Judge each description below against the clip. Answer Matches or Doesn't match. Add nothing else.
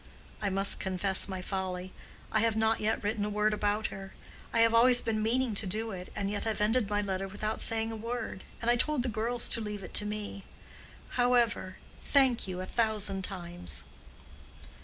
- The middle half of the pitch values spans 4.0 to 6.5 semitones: Doesn't match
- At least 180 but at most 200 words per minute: Matches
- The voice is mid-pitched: Doesn't match